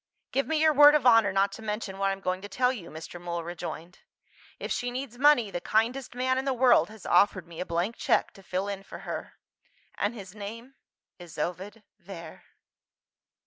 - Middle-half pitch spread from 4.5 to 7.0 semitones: Yes, average, 5.2 semitones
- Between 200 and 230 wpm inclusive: Yes, fast, 205 wpm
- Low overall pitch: No, high, 205 Hz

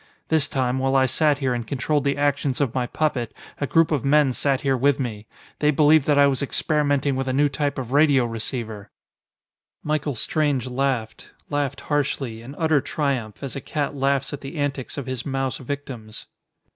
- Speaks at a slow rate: No, average, 190 wpm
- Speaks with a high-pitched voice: No, medium, 140 Hz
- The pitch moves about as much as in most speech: No, narrow, 2.1 semitones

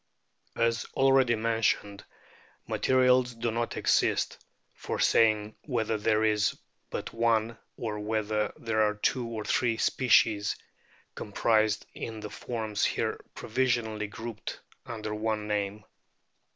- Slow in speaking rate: Yes, slow, 115 wpm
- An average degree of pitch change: No, narrow, 1.6 semitones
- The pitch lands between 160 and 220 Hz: No, low, 110 Hz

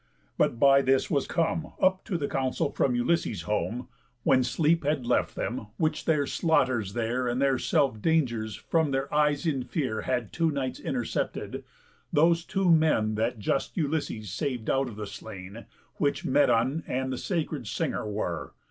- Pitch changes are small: No, average, 5.1 semitones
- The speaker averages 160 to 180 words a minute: Yes, average, 165 wpm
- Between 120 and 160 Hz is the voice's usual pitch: Yes, low, 135 Hz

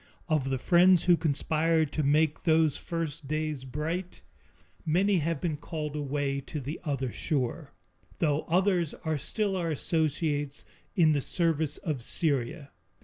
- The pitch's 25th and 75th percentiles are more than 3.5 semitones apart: No, narrow, 2.6 semitones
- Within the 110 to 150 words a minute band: Yes, average, 145 wpm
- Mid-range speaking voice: Yes, medium, 155 Hz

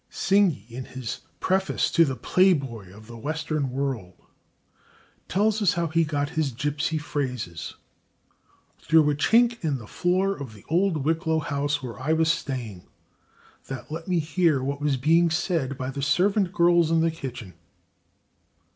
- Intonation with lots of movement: No, average, 4.4 semitones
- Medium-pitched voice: Yes, medium, 150 Hz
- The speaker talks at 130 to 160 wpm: Yes, average, 155 wpm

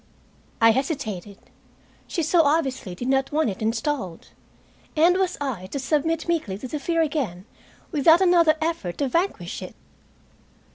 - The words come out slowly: No, average, 145 wpm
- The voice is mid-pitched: No, very high, 285 Hz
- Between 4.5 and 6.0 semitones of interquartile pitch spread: No, wide, 6.6 semitones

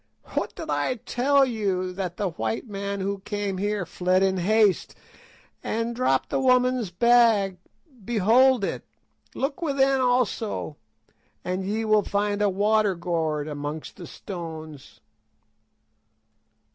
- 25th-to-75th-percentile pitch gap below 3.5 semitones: No, average, 4.5 semitones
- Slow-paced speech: Yes, slow, 120 wpm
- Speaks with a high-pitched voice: Yes, high, 205 Hz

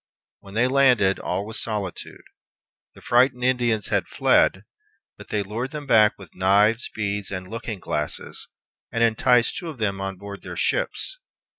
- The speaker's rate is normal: Yes, average, 160 wpm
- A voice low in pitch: Yes, low, 110 Hz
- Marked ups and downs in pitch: No, average, 3.8 semitones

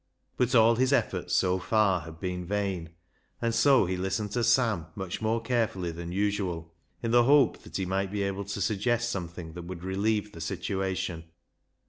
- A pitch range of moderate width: Yes, average, 3.9 semitones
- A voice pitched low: Yes, low, 100 Hz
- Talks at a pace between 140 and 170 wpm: No, average, 180 wpm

